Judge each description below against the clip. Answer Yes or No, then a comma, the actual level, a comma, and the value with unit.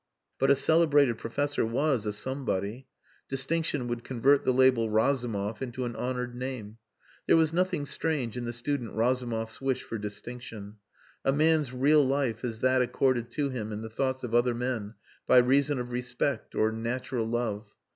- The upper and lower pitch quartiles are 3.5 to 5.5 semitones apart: No, average, 2.9 semitones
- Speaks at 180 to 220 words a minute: No, average, 165 wpm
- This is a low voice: Yes, low, 125 Hz